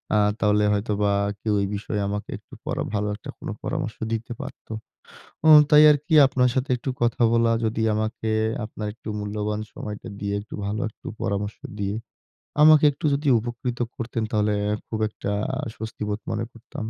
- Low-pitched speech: Yes, low, 110 Hz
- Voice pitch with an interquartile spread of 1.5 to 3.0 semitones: Yes, average, 2.7 semitones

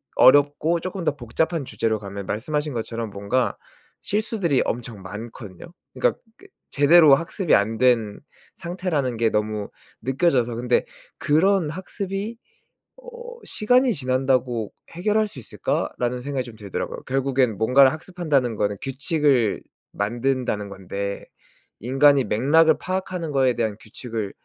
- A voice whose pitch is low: Yes, low, 130 Hz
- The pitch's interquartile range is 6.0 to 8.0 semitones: Yes, wide, 6.6 semitones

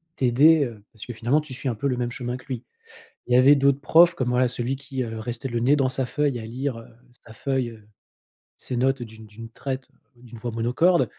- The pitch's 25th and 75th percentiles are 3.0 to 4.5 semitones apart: No, narrow, 2.6 semitones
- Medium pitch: No, low, 125 Hz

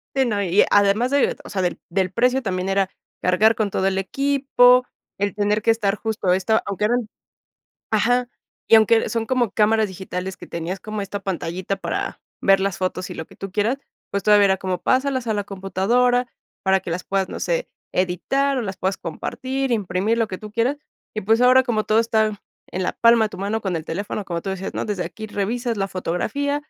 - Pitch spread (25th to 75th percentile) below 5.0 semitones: Yes, average, 3.5 semitones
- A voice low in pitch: No, high, 205 Hz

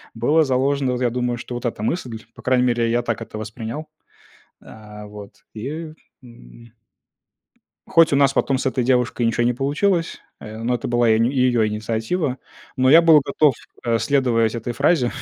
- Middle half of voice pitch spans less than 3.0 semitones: No, average, 3.3 semitones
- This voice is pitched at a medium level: No, low, 125 Hz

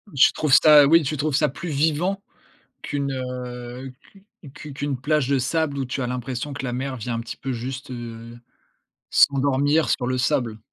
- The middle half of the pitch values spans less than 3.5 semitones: Yes, average, 2.8 semitones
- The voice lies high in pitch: No, low, 135 Hz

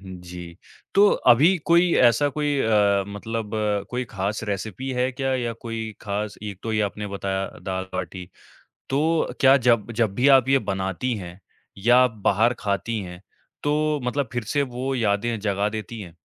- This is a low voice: Yes, low, 110 Hz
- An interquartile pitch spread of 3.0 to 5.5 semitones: Yes, average, 4.5 semitones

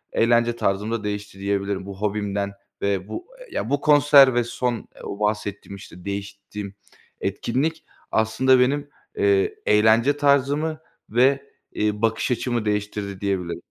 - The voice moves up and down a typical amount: Yes, average, 4.4 semitones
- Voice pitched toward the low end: Yes, low, 105 Hz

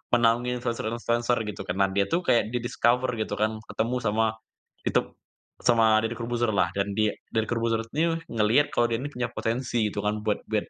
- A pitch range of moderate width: No, narrow, 2.1 semitones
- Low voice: Yes, low, 115 Hz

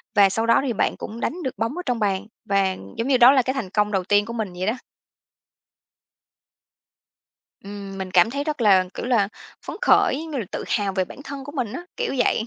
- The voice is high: Yes, high, 225 Hz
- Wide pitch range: No, average, 4.9 semitones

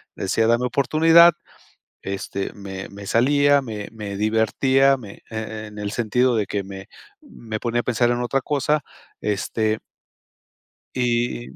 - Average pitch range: Yes, average, 3.8 semitones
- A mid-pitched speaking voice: No, low, 115 Hz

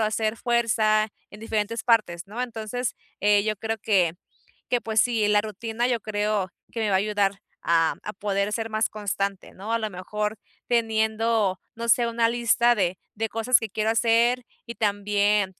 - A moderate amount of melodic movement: No, narrow, 1.9 semitones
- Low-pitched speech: No, high, 215 Hz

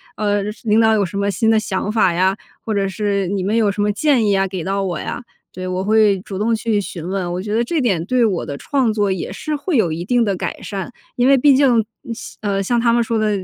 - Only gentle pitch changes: No, average, 3.1 semitones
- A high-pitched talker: Yes, high, 205 Hz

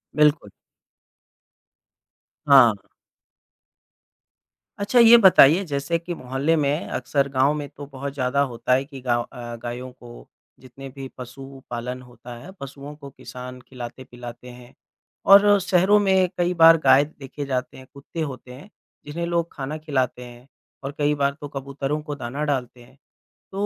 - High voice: No, medium, 140 Hz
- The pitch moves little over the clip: No, average, 3.2 semitones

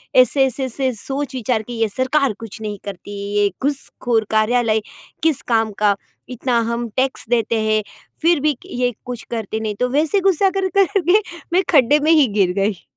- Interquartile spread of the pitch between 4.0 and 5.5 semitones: Yes, average, 4.6 semitones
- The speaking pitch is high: Yes, high, 245 Hz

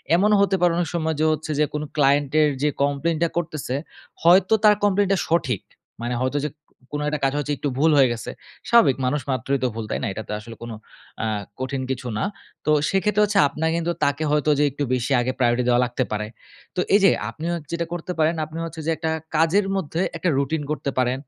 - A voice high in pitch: No, medium, 150 Hz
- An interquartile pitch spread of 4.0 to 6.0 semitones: Yes, average, 4.4 semitones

